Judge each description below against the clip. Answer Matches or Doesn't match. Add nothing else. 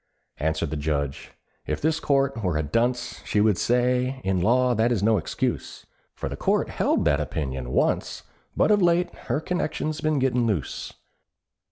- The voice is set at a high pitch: Doesn't match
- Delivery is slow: Doesn't match